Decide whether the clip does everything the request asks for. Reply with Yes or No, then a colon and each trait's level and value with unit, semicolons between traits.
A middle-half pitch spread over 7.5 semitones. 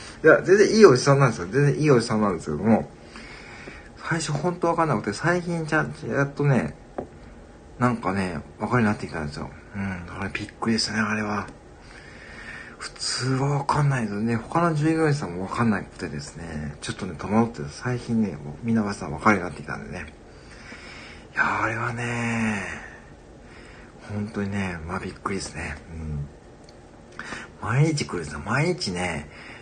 Yes: wide, 8.7 semitones